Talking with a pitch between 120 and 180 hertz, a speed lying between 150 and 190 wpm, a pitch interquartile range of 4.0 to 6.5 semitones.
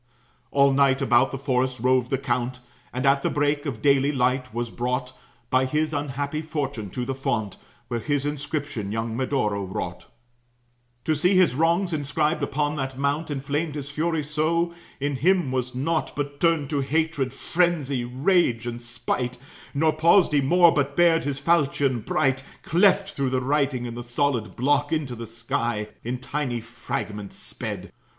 No: medium, 140 Hz; average, 165 wpm; average, 3.2 semitones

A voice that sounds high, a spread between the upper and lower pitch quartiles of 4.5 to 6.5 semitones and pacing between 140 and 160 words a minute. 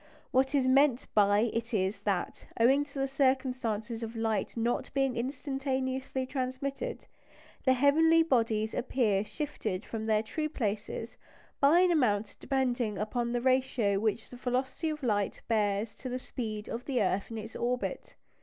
No: high, 245 Hz; average, 3.6 semitones; average, 155 wpm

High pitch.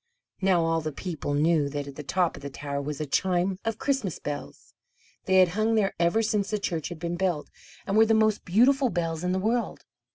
No: medium, 180 Hz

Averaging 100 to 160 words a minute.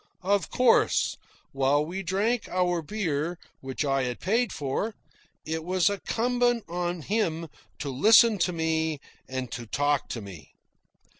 Yes: average, 140 wpm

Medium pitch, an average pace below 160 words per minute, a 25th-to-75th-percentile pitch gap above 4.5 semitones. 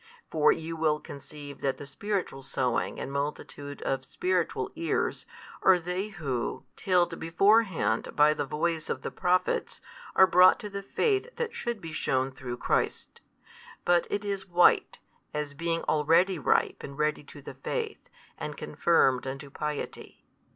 Yes: medium, 160 Hz; average, 150 wpm; average, 5.0 semitones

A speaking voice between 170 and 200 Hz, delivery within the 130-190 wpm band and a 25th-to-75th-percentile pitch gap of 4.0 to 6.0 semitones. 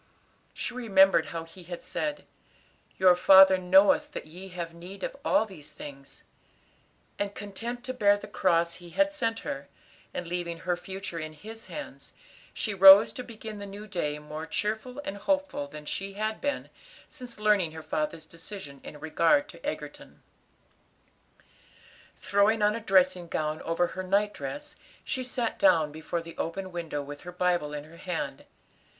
Yes: high, 190 Hz; average, 165 wpm; average, 4.4 semitones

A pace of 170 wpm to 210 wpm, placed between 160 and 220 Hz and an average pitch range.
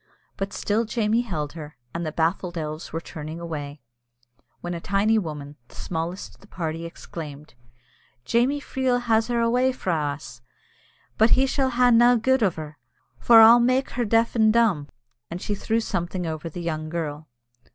No: average, 175 wpm; medium, 185 Hz; wide, 6.6 semitones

